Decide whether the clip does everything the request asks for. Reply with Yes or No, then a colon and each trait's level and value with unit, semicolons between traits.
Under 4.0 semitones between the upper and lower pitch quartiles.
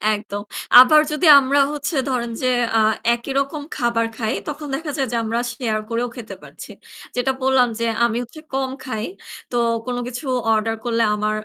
Yes: average, 2.9 semitones